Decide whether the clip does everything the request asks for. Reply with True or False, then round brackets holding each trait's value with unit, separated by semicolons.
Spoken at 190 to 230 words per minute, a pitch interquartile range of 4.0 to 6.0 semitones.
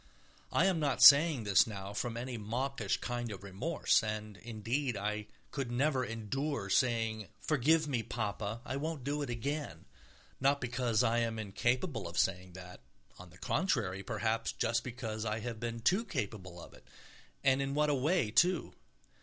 False (165 wpm; 4.5 semitones)